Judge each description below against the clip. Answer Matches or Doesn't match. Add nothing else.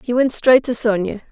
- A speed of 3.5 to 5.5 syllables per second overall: Matches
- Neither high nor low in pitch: Doesn't match